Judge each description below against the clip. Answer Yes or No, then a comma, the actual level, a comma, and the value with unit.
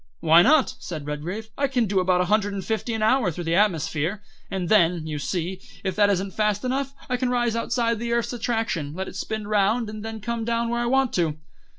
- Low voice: No, high, 210 Hz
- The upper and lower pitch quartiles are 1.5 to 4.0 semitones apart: No, average, 4.5 semitones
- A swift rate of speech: Yes, fast, 230 wpm